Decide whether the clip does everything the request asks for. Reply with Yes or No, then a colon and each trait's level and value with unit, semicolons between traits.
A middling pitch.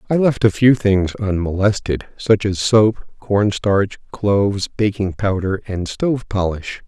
No: low, 100 Hz